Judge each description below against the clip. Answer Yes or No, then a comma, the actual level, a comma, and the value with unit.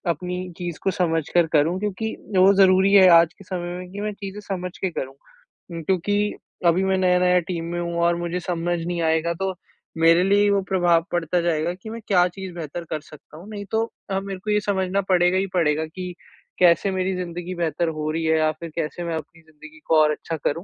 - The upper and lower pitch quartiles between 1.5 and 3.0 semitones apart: Yes, narrow, 2.4 semitones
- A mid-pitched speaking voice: Yes, medium, 175 Hz